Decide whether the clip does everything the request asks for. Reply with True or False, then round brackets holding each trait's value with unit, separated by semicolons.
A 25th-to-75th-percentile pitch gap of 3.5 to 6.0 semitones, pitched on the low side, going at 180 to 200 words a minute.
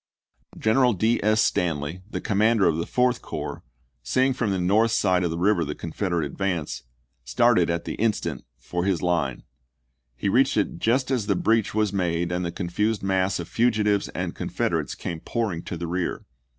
True (4.3 semitones; 95 Hz; 185 wpm)